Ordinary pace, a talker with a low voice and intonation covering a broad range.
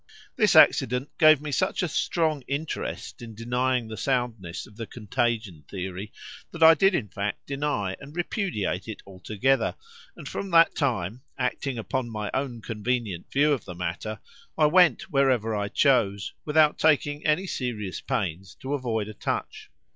Yes: average, 160 wpm; low, 125 Hz; wide, 5.8 semitones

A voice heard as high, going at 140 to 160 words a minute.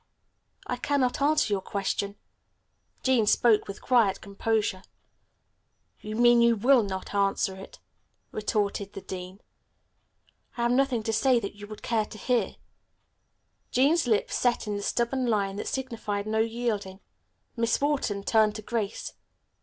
Yes: high, 220 Hz; average, 145 wpm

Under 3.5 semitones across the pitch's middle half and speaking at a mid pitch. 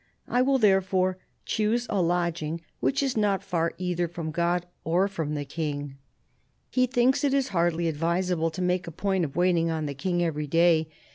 Yes: average, 3.1 semitones; medium, 175 Hz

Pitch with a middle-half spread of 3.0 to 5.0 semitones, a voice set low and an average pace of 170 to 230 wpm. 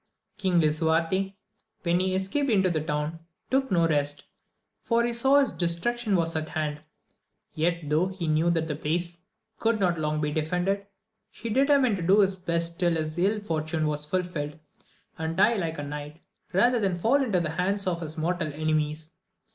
No: average, 3.8 semitones; medium, 170 Hz; average, 180 wpm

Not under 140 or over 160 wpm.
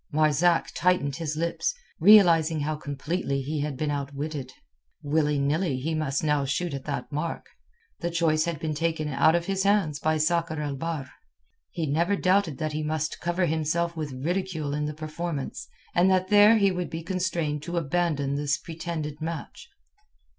No: average, 170 wpm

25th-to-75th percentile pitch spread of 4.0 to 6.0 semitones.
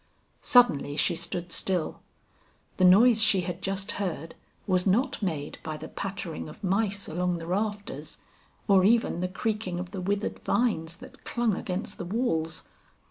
No: average, 3.3 semitones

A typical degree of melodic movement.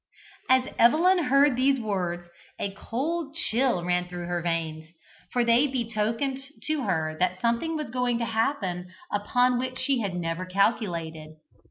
No: wide, 6.6 semitones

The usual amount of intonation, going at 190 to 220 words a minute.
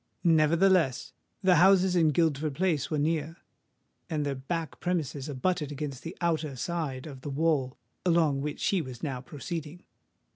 No: average, 3.5 semitones; average, 150 wpm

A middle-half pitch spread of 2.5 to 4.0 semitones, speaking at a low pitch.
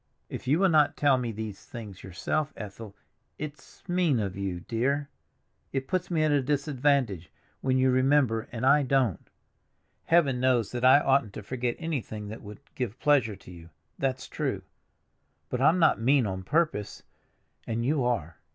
No: average, 5.2 semitones; low, 130 Hz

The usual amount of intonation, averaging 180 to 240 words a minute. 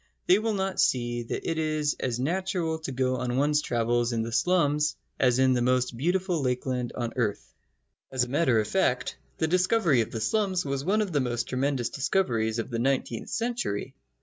No: wide, 5.8 semitones; average, 195 wpm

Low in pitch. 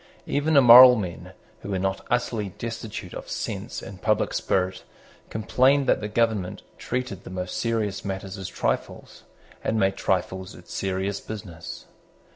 Yes: low, 100 Hz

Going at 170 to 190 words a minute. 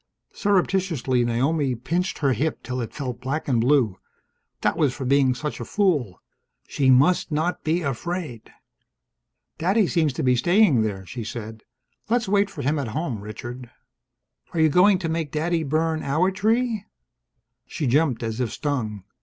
No: average, 160 wpm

